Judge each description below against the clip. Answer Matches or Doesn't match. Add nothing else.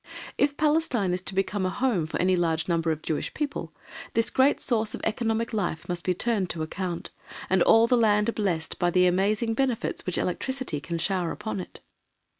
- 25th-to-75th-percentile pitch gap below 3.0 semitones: Doesn't match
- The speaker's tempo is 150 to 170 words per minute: Doesn't match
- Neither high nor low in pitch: Doesn't match